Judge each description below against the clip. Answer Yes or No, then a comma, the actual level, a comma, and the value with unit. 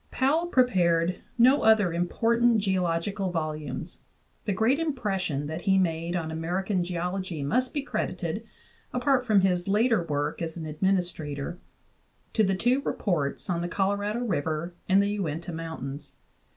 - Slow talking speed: No, average, 145 wpm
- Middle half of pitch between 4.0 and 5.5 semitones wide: Yes, average, 4.7 semitones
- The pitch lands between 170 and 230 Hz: Yes, medium, 185 Hz